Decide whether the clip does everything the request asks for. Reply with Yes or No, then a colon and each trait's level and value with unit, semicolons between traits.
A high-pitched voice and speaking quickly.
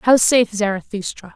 No: high, 210 Hz; slow, 135 wpm